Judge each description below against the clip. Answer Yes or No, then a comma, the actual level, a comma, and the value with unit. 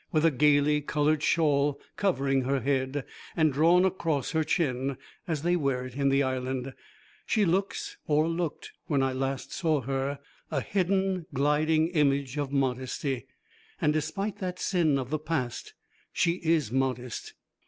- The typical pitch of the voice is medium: Yes, medium, 145 Hz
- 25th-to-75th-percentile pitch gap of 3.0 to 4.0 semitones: Yes, average, 3.5 semitones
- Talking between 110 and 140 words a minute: No, average, 155 wpm